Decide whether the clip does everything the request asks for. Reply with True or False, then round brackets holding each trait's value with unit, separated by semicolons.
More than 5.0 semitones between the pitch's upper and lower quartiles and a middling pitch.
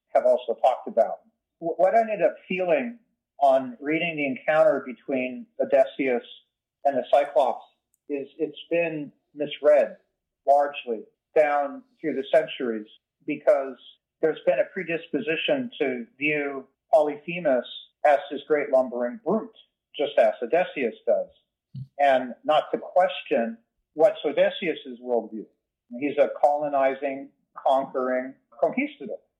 True (5.4 semitones; 145 Hz)